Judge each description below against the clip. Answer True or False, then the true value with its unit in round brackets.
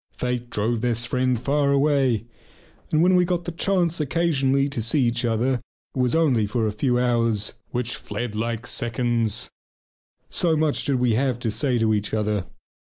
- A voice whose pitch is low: True (125 Hz)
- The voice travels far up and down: False (3.5 semitones)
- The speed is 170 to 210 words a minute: True (180 wpm)